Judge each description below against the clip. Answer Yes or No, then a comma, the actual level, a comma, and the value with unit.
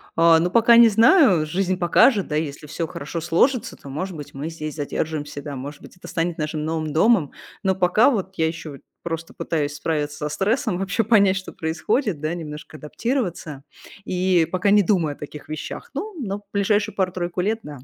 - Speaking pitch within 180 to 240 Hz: No, medium, 170 Hz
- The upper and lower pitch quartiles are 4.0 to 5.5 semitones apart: Yes, average, 4.5 semitones